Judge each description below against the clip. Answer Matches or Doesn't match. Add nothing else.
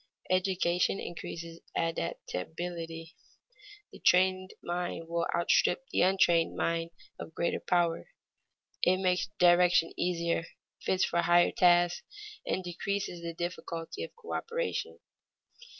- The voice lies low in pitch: Doesn't match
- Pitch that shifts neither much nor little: Doesn't match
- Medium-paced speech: Doesn't match